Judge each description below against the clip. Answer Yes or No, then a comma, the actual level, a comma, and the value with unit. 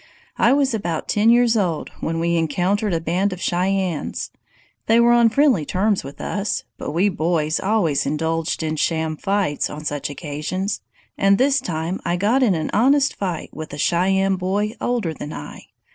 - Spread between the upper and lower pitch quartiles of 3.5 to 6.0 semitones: Yes, average, 4.8 semitones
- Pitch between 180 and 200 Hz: Yes, medium, 185 Hz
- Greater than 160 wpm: Yes, average, 175 wpm